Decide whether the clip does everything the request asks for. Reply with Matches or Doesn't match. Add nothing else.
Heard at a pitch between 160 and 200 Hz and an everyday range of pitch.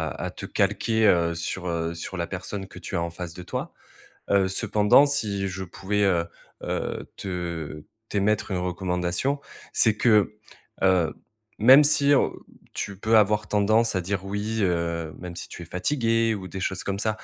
Doesn't match